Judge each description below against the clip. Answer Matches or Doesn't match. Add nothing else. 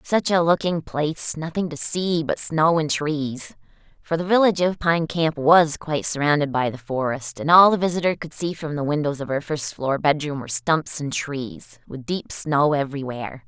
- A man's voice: Doesn't match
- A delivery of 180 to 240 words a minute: Matches